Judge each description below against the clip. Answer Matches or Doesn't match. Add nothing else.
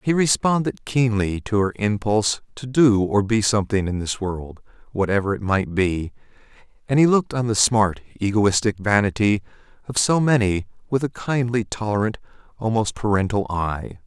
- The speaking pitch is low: Matches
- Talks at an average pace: Matches